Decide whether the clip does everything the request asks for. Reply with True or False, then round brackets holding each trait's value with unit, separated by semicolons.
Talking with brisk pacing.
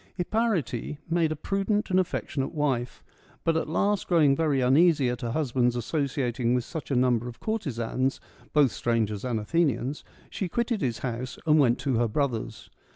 False (170 wpm)